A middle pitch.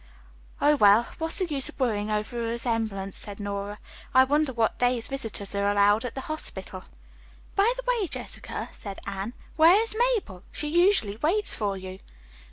No: high, 235 Hz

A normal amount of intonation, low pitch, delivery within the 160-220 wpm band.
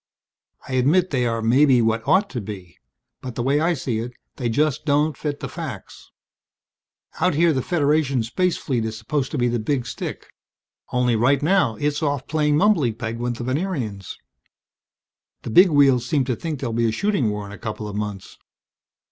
Yes: average, 4.7 semitones; low, 130 Hz; average, 190 wpm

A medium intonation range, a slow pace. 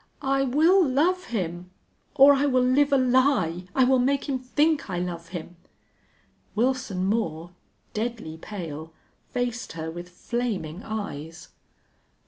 No: wide, 7.2 semitones; slow, 130 wpm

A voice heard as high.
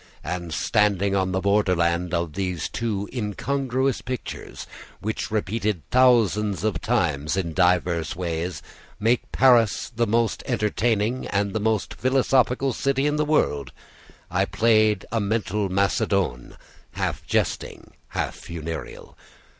No: low, 105 Hz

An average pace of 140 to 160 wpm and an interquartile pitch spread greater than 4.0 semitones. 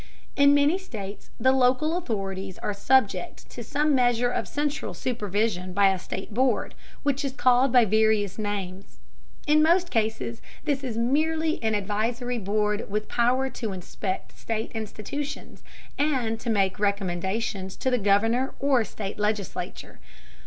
Yes: average, 145 wpm; average, 4.6 semitones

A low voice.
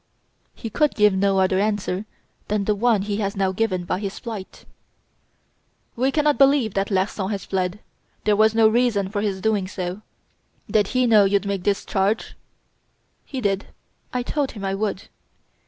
No: high, 205 Hz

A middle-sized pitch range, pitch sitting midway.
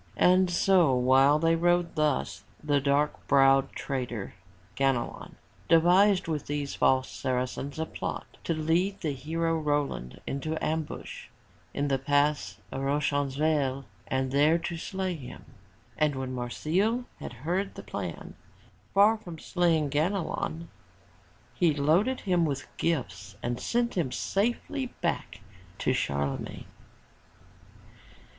Yes: average, 4.3 semitones; medium, 150 Hz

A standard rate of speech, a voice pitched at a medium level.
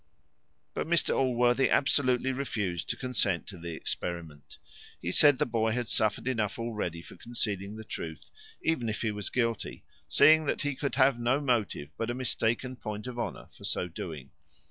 No: average, 175 wpm; low, 115 Hz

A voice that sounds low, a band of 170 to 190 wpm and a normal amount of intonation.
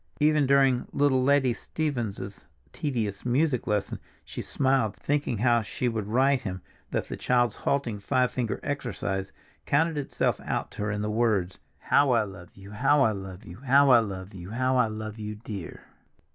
Yes: low, 120 Hz; average, 175 wpm; average, 4.8 semitones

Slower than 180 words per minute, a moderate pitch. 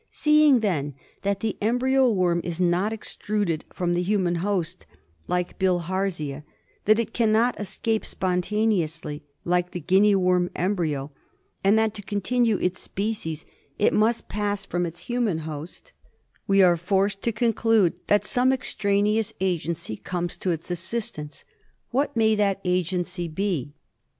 No: average, 140 wpm; high, 195 Hz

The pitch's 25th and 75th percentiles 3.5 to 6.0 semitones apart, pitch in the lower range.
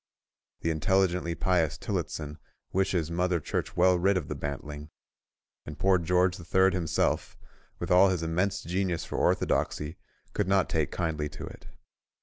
No: narrow, 2.6 semitones; very low, 90 Hz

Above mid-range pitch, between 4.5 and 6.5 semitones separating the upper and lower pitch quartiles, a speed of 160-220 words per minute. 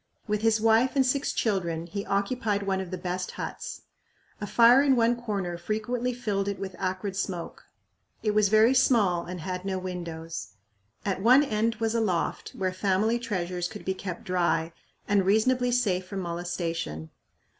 No: high, 200 Hz; average, 3.9 semitones; average, 170 wpm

